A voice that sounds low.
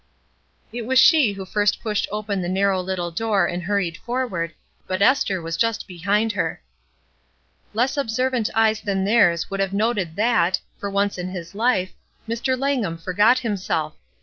No: high, 200 Hz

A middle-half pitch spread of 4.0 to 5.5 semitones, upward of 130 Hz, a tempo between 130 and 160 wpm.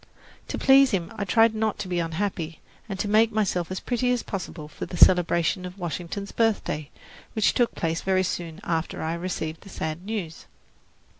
No: average, 4.4 semitones; medium, 185 Hz; average, 180 wpm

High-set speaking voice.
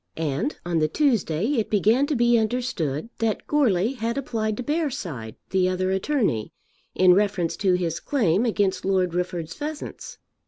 Yes: high, 205 Hz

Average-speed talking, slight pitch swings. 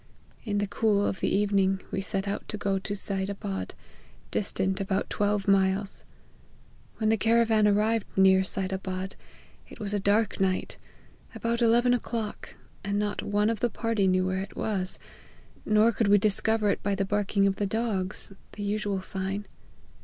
Yes: average, 170 wpm; narrow, 1.8 semitones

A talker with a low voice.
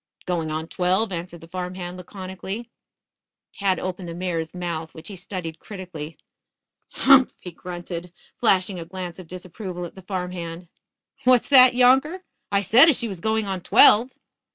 No: medium, 185 Hz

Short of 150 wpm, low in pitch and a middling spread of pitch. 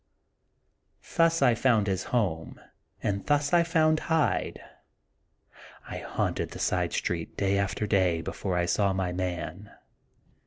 No: average, 140 wpm; low, 100 Hz; wide, 8.0 semitones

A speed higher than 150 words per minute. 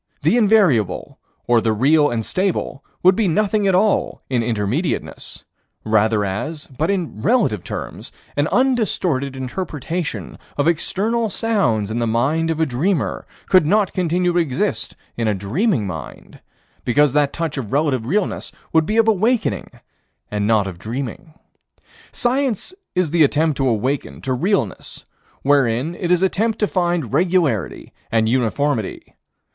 No: average, 145 wpm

